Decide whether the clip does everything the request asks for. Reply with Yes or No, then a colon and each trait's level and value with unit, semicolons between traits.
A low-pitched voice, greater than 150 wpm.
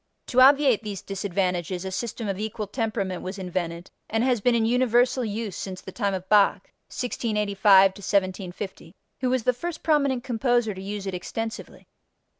No: high, 210 Hz; average, 165 wpm